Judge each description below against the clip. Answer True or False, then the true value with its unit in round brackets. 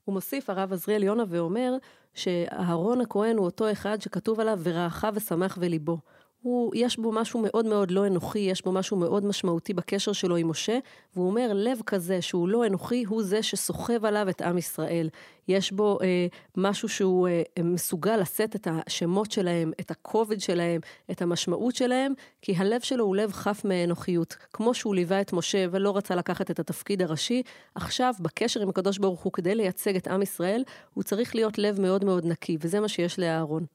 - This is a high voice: True (195 Hz)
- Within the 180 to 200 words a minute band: True (185 wpm)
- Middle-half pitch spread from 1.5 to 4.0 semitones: True (3.5 semitones)